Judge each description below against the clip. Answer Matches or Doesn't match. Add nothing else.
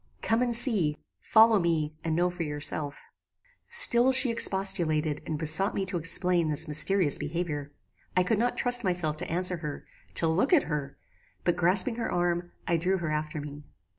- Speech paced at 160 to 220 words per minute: Matches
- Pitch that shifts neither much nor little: Matches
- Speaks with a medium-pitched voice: Matches